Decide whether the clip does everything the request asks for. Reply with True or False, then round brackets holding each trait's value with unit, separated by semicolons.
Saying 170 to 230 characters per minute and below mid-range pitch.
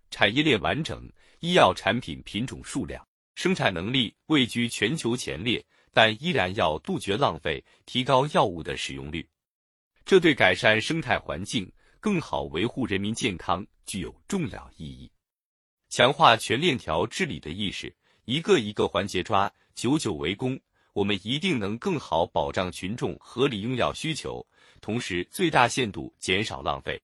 False (240 characters per minute; 110 Hz)